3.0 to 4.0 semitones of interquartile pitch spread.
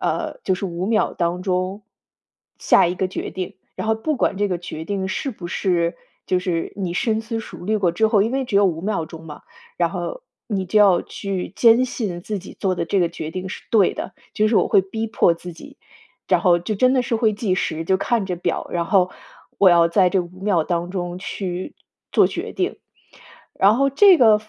Yes: average, 3.6 semitones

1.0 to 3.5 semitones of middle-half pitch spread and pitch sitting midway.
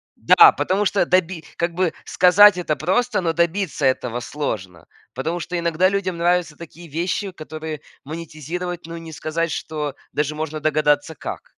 Yes: average, 2.8 semitones; medium, 165 Hz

